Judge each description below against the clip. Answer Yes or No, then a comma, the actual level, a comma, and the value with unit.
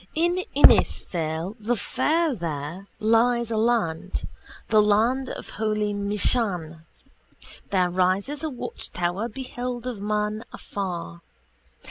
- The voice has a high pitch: Yes, high, 210 Hz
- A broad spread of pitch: No, average, 5.0 semitones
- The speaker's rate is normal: No, slow, 105 wpm